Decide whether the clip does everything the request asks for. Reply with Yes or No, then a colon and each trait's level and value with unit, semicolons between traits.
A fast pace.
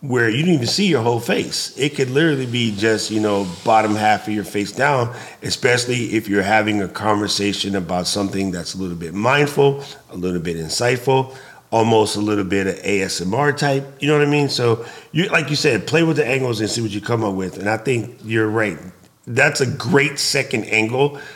Yes: fast, 215 wpm